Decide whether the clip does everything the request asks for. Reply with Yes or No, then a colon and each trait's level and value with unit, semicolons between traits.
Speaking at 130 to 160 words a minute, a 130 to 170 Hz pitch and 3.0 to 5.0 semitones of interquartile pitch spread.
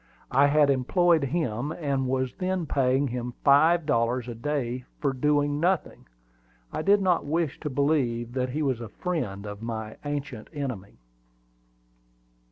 Yes: average, 150 wpm; medium, 140 Hz; average, 3.8 semitones